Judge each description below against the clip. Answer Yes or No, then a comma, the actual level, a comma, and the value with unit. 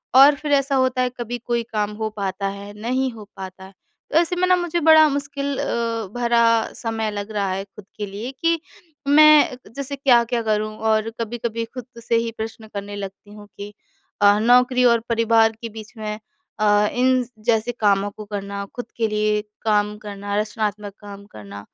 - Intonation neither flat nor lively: Yes, average, 3.3 semitones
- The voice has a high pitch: Yes, high, 225 Hz